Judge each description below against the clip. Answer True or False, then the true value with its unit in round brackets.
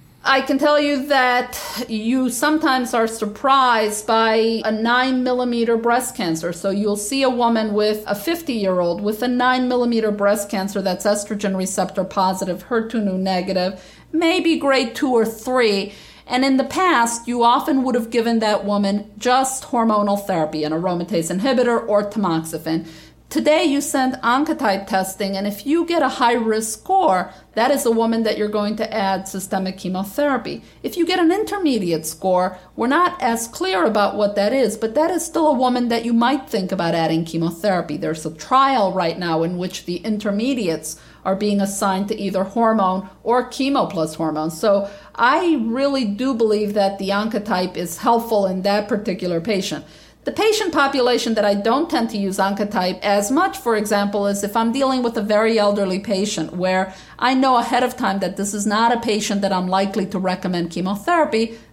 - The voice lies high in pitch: True (215 Hz)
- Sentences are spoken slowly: False (180 wpm)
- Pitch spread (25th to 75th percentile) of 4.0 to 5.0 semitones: True (4.6 semitones)